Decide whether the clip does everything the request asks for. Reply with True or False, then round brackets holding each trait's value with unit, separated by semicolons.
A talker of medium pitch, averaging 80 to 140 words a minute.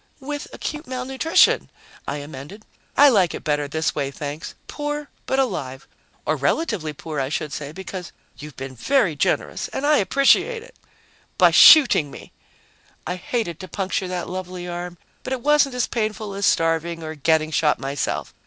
False (180 Hz; 165 wpm)